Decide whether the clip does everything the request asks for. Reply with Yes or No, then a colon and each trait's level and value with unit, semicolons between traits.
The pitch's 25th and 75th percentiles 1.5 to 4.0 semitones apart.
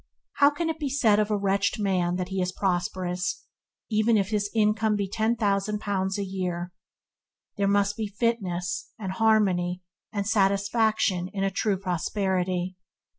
Yes: narrow, 2.6 semitones